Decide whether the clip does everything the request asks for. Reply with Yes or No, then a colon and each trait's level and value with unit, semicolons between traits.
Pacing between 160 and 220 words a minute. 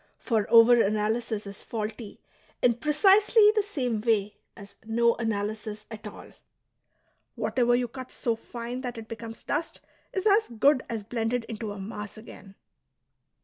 No: average, 145 wpm